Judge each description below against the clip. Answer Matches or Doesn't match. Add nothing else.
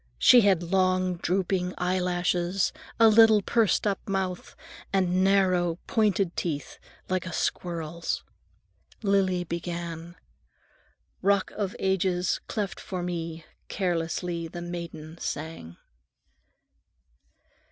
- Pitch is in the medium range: Matches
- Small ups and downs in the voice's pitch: Matches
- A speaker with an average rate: Doesn't match